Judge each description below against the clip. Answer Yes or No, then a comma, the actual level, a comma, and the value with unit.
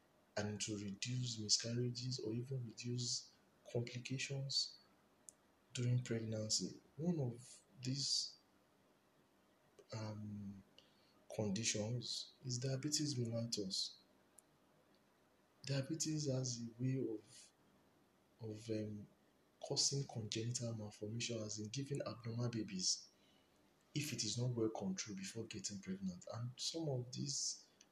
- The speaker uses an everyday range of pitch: Yes, average, 3.6 semitones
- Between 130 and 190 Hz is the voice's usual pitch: No, low, 120 Hz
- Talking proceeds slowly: Yes, slow, 100 wpm